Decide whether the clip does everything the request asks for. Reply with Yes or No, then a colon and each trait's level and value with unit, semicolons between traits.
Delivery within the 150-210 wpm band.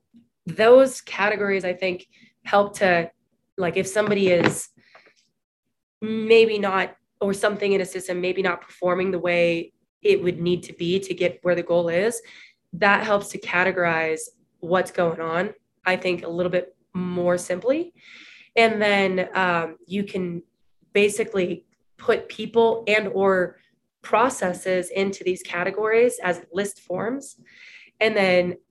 No: average, 140 wpm